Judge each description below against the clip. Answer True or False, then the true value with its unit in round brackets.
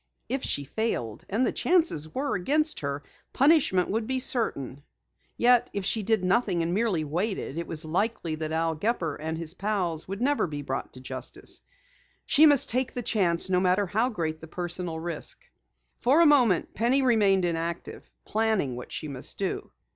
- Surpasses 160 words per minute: True (175 wpm)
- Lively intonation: True (6.6 semitones)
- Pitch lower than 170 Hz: False (185 Hz)